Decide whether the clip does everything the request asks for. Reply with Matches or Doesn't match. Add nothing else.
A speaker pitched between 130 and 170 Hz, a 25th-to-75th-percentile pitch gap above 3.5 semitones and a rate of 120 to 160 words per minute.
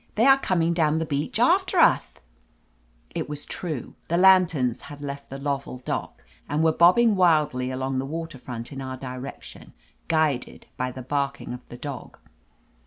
Doesn't match